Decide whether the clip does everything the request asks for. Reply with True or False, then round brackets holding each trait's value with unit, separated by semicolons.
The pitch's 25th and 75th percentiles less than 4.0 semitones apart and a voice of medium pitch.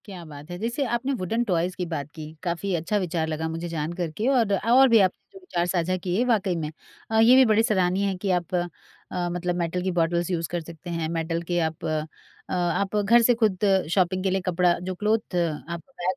True (3.6 semitones; 180 Hz)